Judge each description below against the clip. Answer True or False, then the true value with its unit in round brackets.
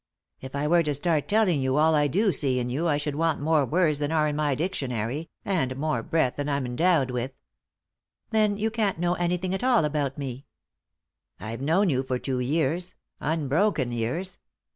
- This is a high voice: False (150 Hz)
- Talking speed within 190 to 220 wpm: True (205 wpm)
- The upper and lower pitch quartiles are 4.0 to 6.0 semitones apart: True (4.8 semitones)